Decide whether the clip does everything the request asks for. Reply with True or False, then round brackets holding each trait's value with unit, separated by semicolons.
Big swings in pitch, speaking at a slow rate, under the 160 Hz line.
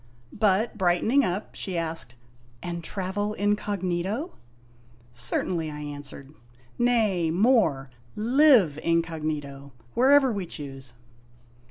False (5.8 semitones; 90 wpm; 180 Hz)